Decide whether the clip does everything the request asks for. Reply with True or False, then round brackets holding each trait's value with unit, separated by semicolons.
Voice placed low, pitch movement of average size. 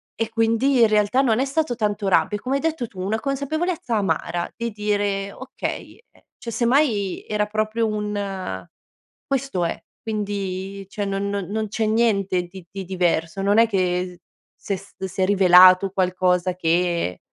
False (205 Hz; 3.4 semitones)